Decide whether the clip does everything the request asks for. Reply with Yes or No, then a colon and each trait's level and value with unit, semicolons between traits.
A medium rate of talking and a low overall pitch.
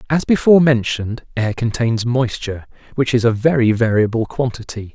Yes: average, 145 wpm; low, 120 Hz